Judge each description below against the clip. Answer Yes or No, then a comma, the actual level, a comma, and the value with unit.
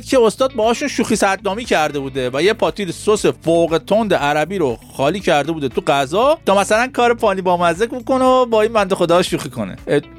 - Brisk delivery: Yes, fast, 195 wpm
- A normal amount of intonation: No, wide, 6.0 semitones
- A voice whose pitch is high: Yes, high, 200 Hz